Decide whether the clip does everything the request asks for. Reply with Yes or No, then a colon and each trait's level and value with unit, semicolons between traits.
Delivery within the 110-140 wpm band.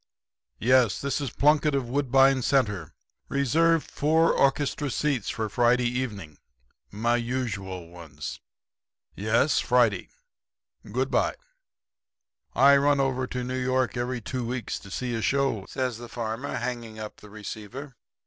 Yes: slow, 135 wpm